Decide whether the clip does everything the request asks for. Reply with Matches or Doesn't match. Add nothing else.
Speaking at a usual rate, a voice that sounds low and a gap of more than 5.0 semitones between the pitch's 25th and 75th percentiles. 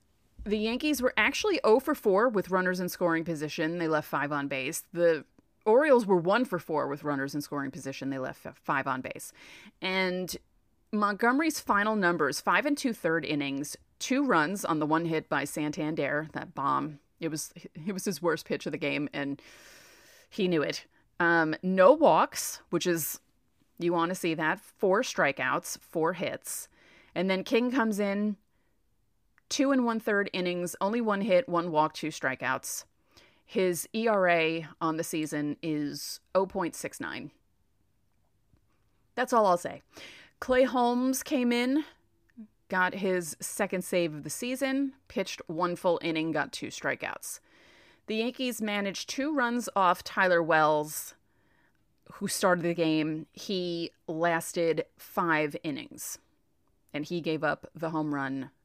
Doesn't match